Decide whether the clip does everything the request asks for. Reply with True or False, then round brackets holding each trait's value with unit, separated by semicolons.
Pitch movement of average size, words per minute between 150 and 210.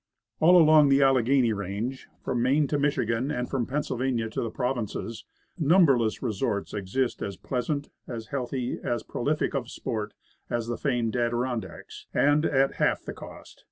True (3.4 semitones; 160 wpm)